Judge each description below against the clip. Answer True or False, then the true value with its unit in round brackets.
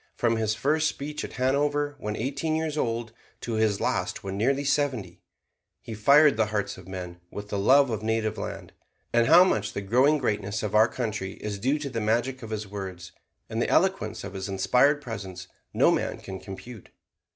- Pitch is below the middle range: True (110 Hz)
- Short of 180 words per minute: False (195 wpm)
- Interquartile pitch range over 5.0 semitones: True (5.4 semitones)